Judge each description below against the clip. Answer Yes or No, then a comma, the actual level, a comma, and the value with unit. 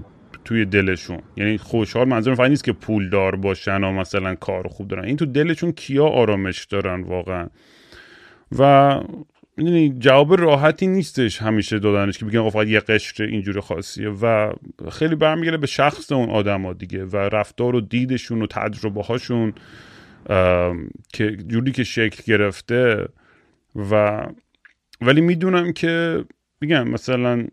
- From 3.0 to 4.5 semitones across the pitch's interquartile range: No, average, 5.2 semitones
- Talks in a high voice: No, low, 110 Hz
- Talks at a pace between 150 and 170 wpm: No, average, 140 wpm